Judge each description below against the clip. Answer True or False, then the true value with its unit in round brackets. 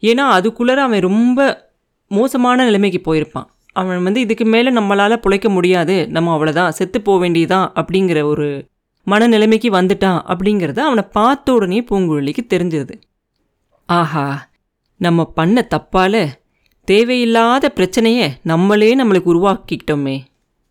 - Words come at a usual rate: True (110 wpm)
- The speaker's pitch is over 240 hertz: False (190 Hz)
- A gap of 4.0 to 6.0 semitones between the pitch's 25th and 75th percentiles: True (5.5 semitones)